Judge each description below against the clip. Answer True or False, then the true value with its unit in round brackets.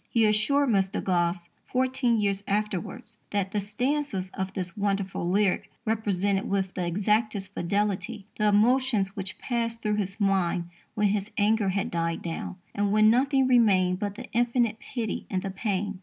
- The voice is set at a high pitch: True (205 Hz)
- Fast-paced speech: False (160 wpm)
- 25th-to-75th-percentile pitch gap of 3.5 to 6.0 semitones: False (2.8 semitones)